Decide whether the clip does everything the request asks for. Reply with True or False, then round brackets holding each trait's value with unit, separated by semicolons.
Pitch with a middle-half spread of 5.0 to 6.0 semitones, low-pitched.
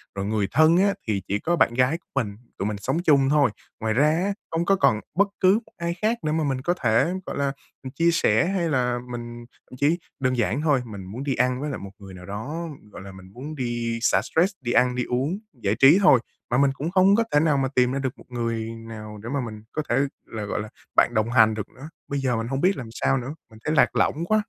True (5.6 semitones; 130 Hz)